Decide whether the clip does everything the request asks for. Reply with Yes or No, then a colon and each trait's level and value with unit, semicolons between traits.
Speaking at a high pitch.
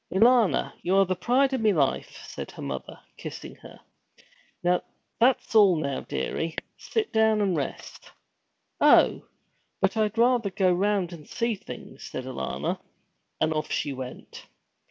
Yes: high, 195 Hz